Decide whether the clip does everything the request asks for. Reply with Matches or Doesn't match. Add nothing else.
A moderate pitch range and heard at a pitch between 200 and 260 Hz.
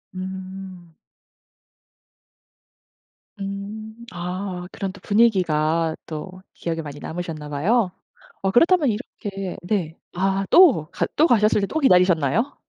Doesn't match